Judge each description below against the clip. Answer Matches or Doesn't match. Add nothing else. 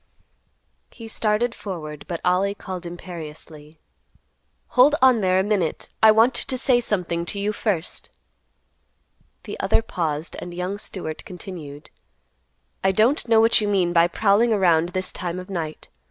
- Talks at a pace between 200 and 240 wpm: Doesn't match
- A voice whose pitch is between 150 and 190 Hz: Matches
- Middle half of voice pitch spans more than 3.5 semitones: Matches